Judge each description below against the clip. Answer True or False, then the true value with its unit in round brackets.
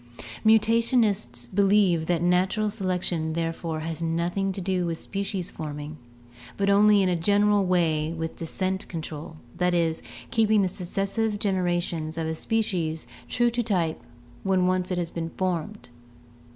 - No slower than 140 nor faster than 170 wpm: True (145 wpm)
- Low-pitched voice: False (180 Hz)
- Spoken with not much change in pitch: False (3.5 semitones)